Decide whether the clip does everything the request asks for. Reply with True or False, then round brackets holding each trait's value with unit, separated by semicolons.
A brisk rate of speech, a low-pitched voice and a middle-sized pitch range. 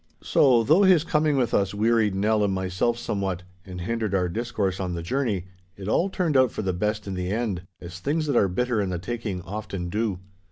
True (215 wpm; 105 Hz; 4.3 semitones)